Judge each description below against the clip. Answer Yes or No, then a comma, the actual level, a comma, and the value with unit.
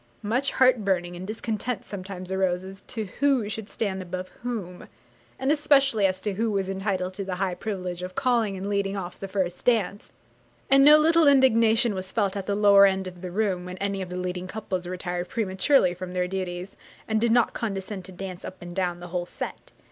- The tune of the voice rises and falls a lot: No, average, 3.2 semitones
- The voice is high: Yes, high, 195 Hz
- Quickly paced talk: Yes, fast, 210 wpm